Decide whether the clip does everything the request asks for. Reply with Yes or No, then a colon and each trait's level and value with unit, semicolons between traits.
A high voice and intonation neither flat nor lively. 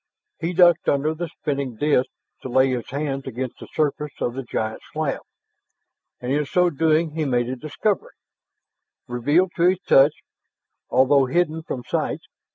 No: medium, 145 Hz; average, 3.5 semitones